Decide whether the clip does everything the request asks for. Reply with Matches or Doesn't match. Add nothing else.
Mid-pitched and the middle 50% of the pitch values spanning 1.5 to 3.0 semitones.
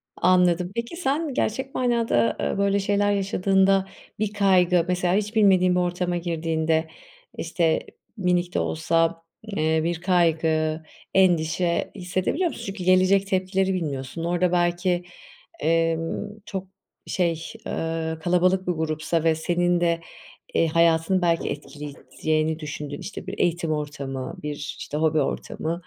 Matches